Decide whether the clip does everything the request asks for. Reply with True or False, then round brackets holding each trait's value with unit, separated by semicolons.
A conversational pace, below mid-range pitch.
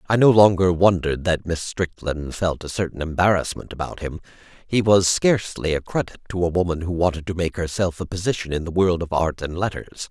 False (210 wpm; 90 Hz)